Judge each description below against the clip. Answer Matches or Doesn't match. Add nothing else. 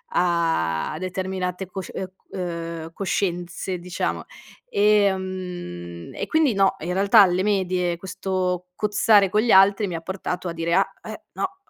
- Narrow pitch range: Matches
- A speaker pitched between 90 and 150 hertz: Doesn't match